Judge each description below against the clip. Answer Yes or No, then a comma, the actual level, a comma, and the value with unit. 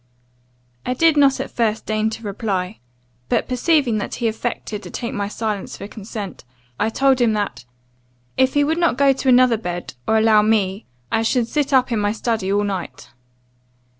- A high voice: Yes, high, 225 Hz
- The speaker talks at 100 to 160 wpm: No, average, 185 wpm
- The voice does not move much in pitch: No, average, 3.7 semitones